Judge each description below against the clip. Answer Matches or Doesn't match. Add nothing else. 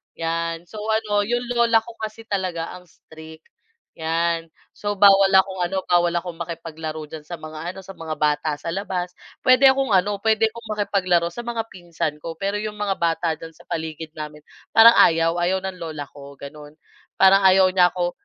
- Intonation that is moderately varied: Matches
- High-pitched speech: Doesn't match